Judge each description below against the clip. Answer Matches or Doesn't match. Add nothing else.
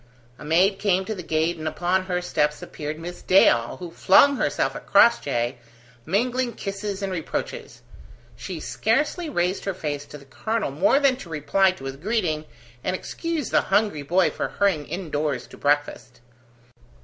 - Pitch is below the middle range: Doesn't match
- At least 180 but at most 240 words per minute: Doesn't match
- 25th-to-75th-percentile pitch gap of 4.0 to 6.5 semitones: Matches